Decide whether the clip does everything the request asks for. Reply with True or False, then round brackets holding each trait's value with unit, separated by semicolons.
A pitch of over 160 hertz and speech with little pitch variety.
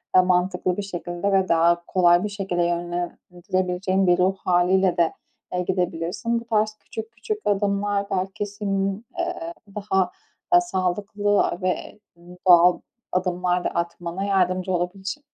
True (185 Hz; 2.1 semitones)